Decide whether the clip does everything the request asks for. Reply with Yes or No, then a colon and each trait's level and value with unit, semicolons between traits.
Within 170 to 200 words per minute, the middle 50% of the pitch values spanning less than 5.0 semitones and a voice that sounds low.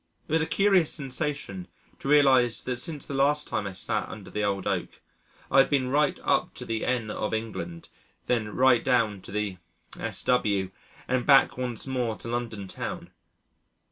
Yes: average, 175 wpm; average, 4.5 semitones; low, 125 Hz